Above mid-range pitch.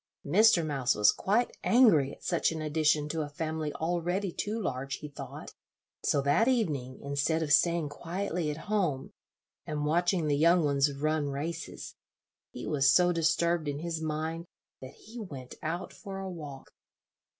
No: medium, 160 Hz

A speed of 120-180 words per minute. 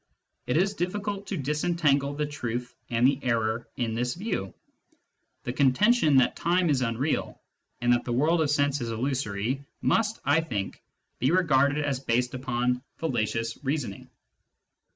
Yes: average, 150 wpm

